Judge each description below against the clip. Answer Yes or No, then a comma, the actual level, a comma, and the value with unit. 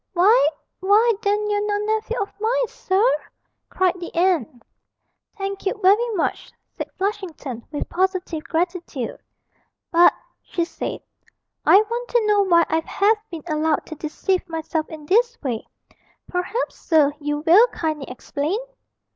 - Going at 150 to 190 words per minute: No, average, 140 wpm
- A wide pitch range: No, average, 4.7 semitones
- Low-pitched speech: No, very high, 370 Hz